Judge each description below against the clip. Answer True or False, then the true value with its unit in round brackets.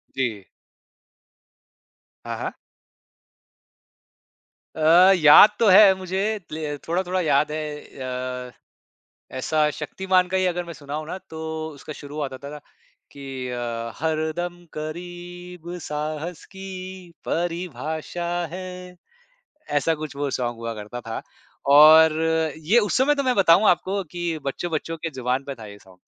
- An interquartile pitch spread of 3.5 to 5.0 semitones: True (4.0 semitones)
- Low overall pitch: False (155 Hz)